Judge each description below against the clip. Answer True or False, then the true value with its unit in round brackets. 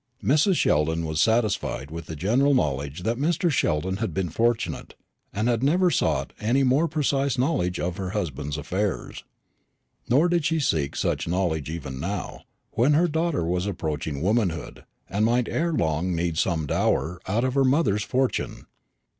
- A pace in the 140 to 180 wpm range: True (165 wpm)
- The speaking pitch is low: True (100 Hz)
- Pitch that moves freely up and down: True (8.6 semitones)